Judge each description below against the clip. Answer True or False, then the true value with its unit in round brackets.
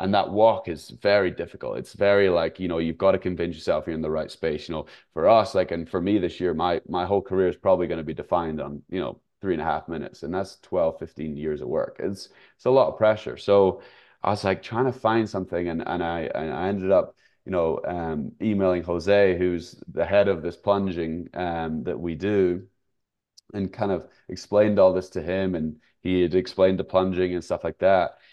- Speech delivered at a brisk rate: True (235 wpm)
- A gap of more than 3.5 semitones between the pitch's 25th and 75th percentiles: False (2.8 semitones)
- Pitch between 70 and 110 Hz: True (95 Hz)